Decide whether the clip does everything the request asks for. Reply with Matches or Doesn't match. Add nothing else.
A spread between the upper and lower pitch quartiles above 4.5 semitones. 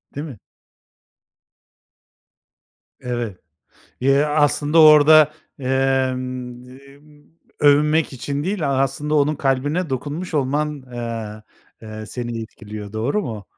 Doesn't match